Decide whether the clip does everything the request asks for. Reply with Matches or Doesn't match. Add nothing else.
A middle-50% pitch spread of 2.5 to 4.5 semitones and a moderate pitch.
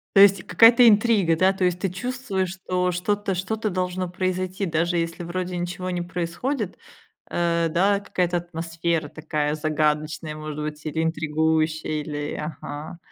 Matches